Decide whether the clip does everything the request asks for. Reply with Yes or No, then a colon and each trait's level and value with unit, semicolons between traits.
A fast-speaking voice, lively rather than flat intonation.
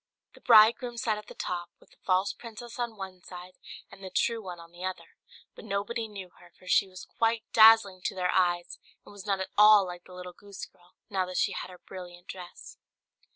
No: fast, 220 wpm; average, 3.1 semitones